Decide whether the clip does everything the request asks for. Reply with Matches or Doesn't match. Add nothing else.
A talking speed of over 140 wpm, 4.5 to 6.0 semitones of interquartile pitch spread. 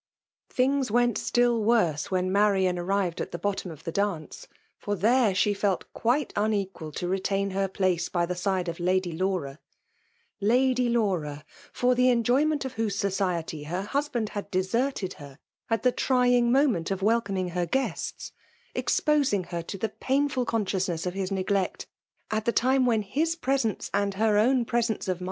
Matches